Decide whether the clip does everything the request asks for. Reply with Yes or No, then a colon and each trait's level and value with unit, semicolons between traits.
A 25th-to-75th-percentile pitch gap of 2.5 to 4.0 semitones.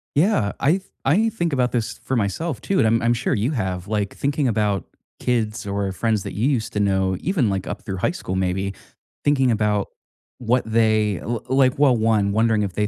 No: average, 4.5 semitones